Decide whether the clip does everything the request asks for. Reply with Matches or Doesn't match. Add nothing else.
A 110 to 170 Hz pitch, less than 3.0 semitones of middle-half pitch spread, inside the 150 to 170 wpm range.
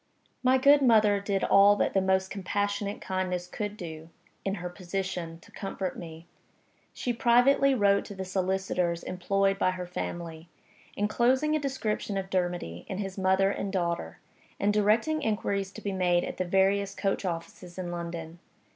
Doesn't match